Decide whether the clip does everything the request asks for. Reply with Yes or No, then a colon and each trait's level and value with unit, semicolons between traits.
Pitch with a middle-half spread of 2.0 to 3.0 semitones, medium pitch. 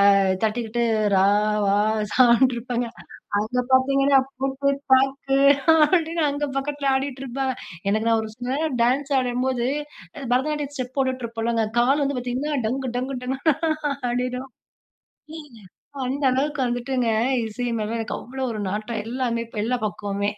No: narrow, 2.6 semitones; very high, 255 Hz